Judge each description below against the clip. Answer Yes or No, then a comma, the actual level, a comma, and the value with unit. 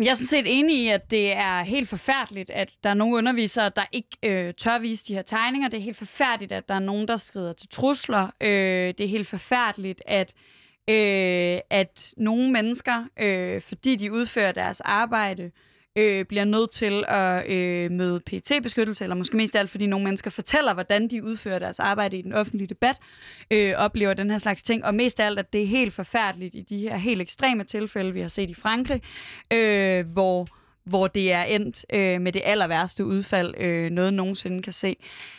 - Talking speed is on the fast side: No, average, 205 wpm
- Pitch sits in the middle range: No, high, 205 Hz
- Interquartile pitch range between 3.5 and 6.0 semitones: No, average, 2.9 semitones